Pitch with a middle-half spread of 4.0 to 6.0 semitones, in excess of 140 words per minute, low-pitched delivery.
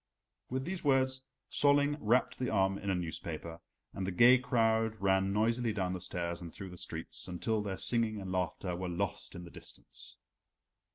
Yes: average, 4.8 semitones; average, 180 wpm; low, 100 Hz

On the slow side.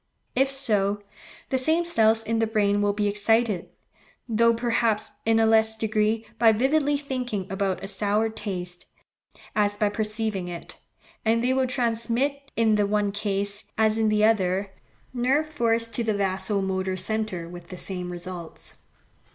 No: average, 160 wpm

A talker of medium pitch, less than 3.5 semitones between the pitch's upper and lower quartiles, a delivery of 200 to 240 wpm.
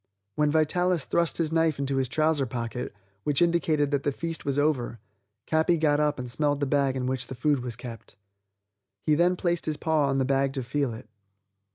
Yes: medium, 145 Hz; average, 3.1 semitones; fast, 205 wpm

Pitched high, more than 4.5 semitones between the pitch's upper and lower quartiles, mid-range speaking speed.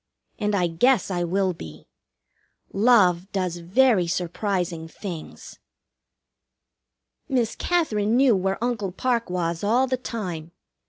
No: high, 195 Hz; average, 5.0 semitones; slow, 115 wpm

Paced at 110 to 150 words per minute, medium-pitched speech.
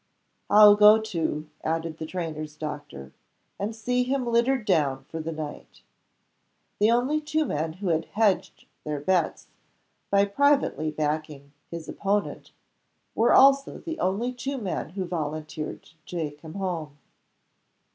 Yes: slow, 135 wpm; medium, 180 Hz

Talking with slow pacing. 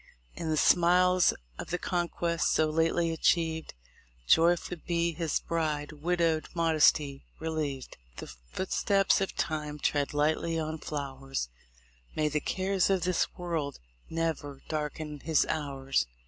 Yes: slow, 125 wpm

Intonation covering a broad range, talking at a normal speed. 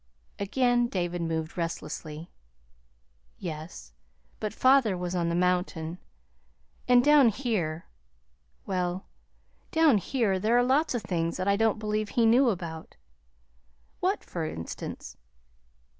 No: wide, 6.0 semitones; slow, 120 wpm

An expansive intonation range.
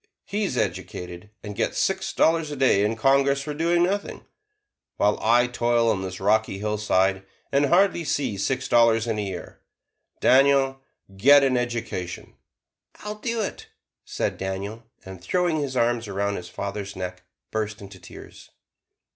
Yes: wide, 5.7 semitones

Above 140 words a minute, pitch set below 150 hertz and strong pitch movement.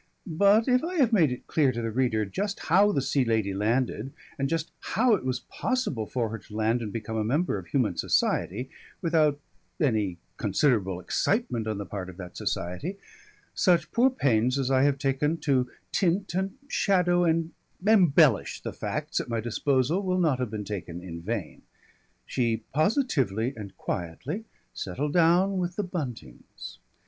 Yes: average, 170 wpm; low, 135 Hz; wide, 8.3 semitones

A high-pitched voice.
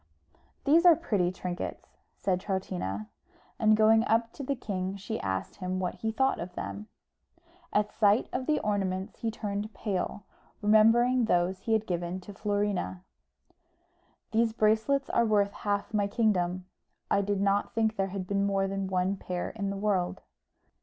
Yes: high, 205 Hz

